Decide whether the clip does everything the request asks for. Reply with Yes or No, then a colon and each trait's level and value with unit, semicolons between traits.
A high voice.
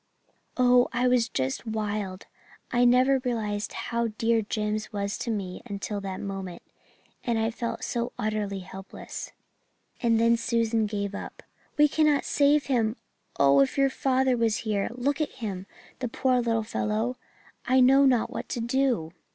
Yes: high, 230 Hz